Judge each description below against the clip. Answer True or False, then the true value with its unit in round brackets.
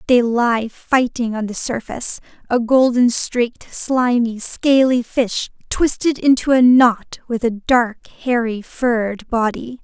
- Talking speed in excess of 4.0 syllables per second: False (3.9 syllables/s)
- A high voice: True (240 Hz)